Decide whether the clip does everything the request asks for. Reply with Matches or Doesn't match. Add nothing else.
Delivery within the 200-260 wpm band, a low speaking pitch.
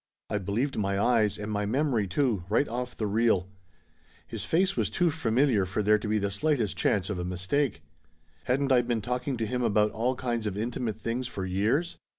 Matches